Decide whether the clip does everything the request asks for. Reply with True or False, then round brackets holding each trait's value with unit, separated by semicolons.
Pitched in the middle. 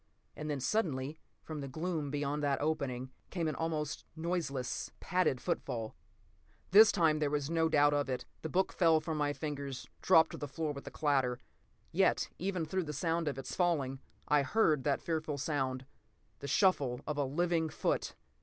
True (150 Hz)